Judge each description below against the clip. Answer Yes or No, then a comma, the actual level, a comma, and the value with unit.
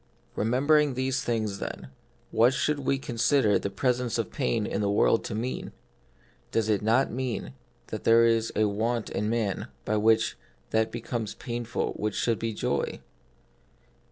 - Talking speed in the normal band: Yes, average, 155 wpm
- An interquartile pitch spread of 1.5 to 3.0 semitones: Yes, narrow, 2.6 semitones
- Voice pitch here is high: No, low, 115 Hz